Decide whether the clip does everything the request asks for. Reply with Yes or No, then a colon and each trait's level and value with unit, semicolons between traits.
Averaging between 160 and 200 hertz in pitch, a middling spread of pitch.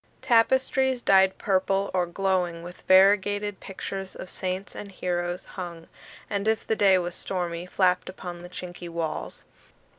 No: medium, 185 Hz; narrow, 2.1 semitones